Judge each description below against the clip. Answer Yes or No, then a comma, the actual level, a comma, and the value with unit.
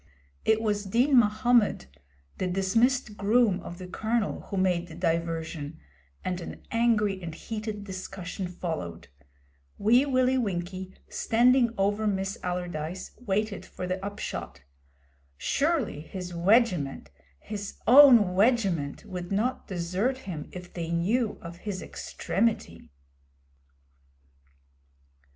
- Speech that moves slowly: Yes, slow, 110 wpm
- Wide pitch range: No, average, 4.4 semitones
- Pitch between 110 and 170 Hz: No, high, 195 Hz